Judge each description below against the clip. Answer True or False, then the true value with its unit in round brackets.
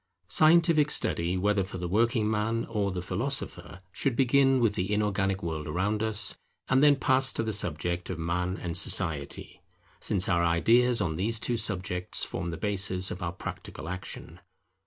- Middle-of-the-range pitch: False (100 Hz)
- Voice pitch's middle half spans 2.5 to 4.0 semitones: False (4.5 semitones)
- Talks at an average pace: True (170 wpm)